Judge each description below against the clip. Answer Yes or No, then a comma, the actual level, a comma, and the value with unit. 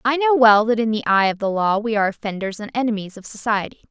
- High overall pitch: Yes, high, 220 Hz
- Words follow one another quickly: Yes, fast, 260 wpm